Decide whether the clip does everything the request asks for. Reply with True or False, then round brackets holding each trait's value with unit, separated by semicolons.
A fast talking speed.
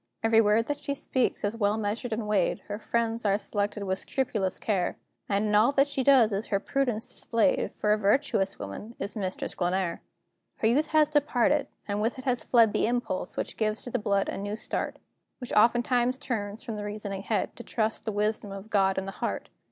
True (215 wpm)